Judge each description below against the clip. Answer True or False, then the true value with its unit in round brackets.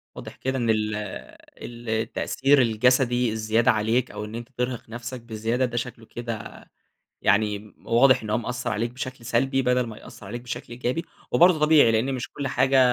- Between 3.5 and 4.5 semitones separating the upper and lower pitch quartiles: False (2.4 semitones)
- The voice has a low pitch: True (120 Hz)